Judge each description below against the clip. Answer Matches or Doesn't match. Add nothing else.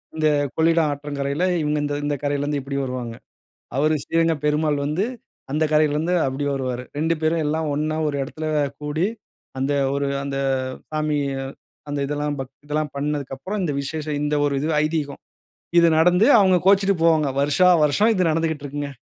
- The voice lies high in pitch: Doesn't match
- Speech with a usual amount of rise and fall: Doesn't match